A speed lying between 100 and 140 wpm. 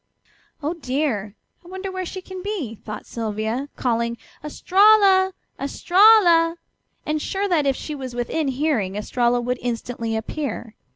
Yes: slow, 135 wpm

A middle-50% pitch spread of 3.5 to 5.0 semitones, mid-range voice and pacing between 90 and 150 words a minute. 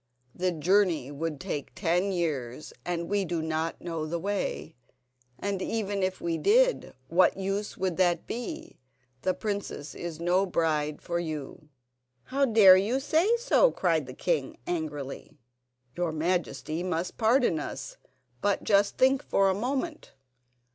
Yes: average, 4.1 semitones; medium, 180 Hz; average, 145 wpm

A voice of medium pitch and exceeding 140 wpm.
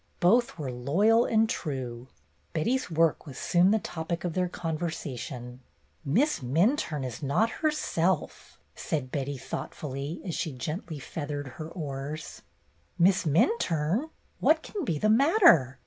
No: medium, 160 Hz; slow, 135 wpm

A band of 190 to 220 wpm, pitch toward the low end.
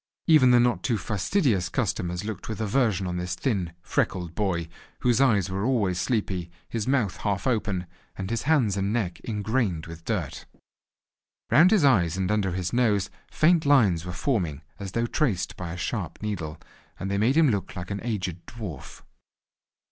No: average, 175 wpm; low, 100 Hz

